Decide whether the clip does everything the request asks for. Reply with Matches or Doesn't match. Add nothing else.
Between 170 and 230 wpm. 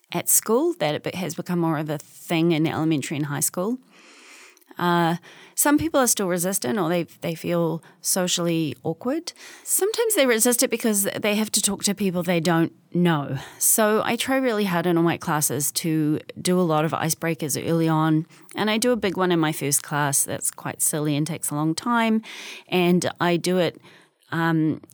Matches